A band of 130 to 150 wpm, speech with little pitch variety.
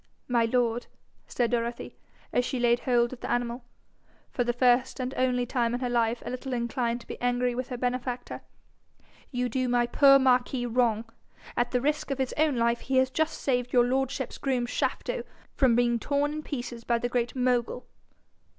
No: average, 190 wpm; narrow, 1.3 semitones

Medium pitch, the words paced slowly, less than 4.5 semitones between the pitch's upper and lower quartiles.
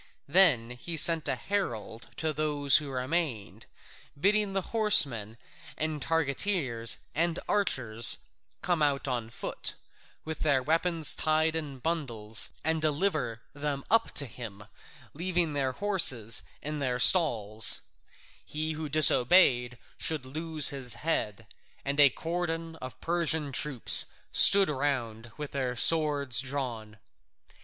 No: medium, 145 Hz; slow, 125 wpm; average, 4.8 semitones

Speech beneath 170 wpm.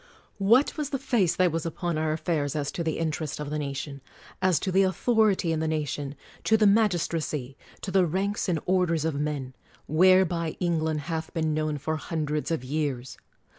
No: average, 195 wpm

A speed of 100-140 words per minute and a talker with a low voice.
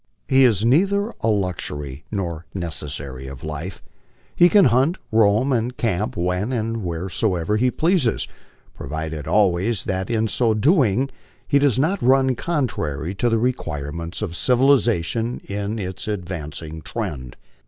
Yes: slow, 135 wpm; low, 105 Hz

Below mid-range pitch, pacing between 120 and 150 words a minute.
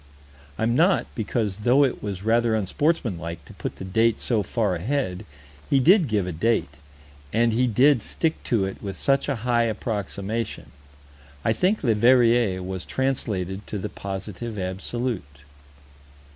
Yes: low, 110 Hz; average, 145 wpm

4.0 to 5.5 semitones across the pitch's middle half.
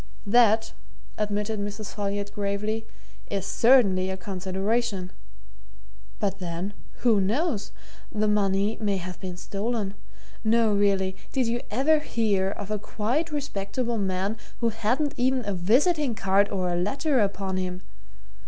No: average, 3.1 semitones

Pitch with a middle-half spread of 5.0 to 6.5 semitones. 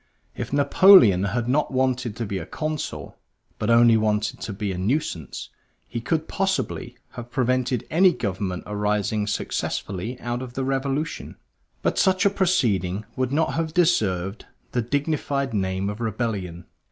Yes: wide, 5.5 semitones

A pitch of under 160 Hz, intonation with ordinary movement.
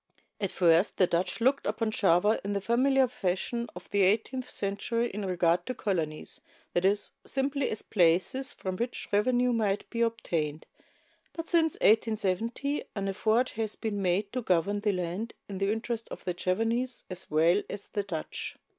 No: high, 205 Hz; average, 4.2 semitones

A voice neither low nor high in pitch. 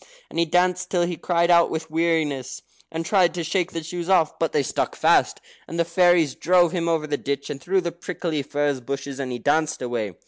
Yes: medium, 165 Hz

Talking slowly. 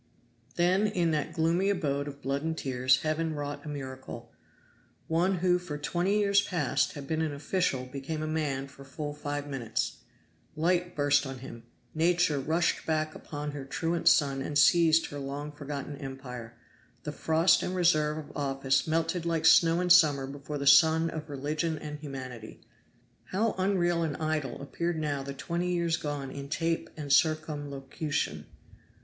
No: average, 165 wpm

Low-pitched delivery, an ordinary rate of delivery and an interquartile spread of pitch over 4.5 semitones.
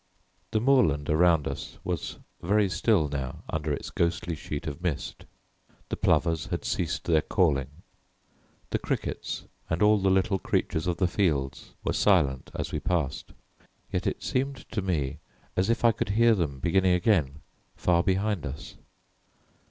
Yes: very low, 85 Hz; average, 155 wpm; average, 5.3 semitones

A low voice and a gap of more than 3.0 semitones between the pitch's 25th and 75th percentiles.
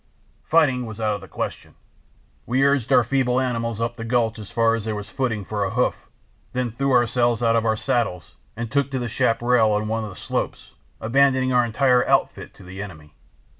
No: low, 115 Hz; narrow, 2.6 semitones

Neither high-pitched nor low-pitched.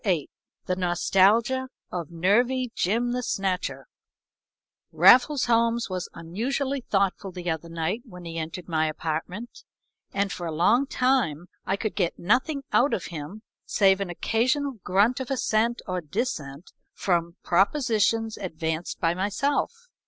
No: high, 195 Hz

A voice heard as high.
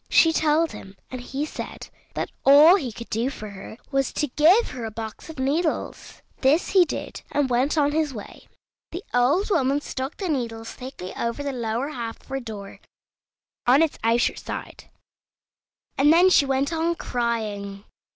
Yes: very high, 270 Hz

